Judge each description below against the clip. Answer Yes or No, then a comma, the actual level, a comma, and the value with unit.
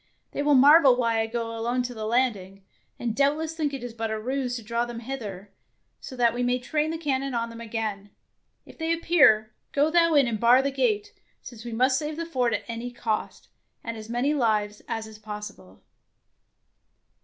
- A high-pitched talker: Yes, high, 240 Hz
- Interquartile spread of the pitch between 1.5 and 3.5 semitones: No, average, 3.9 semitones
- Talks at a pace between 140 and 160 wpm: No, average, 200 wpm